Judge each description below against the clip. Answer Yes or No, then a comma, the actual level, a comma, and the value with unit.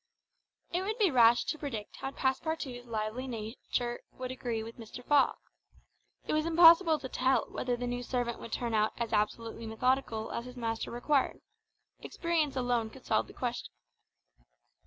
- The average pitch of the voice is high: Yes, high, 245 Hz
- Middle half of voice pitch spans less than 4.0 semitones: Yes, average, 3.1 semitones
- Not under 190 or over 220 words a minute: No, average, 160 wpm